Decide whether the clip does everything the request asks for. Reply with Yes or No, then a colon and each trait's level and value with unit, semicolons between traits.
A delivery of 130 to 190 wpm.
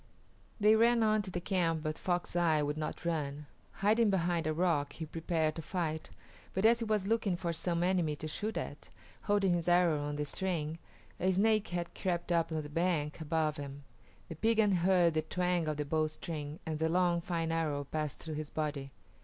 No: average, 200 wpm